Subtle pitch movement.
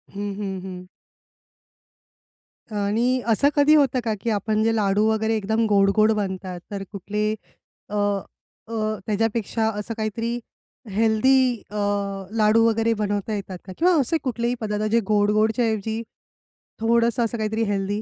Yes: narrow, 1.9 semitones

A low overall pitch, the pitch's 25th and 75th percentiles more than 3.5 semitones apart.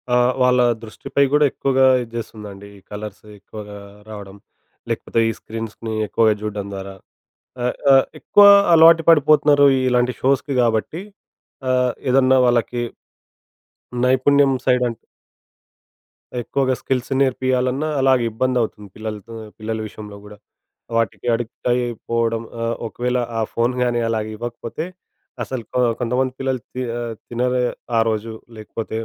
No: low, 120 Hz; average, 2.8 semitones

